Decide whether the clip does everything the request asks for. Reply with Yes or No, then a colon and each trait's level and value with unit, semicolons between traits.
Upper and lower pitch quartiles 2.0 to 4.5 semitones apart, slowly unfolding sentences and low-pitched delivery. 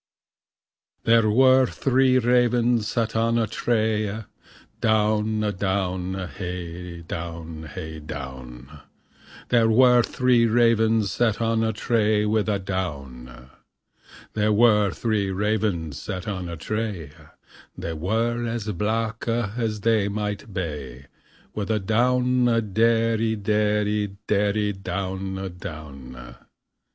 Yes: average, 3.9 semitones; slow, 115 wpm; low, 105 Hz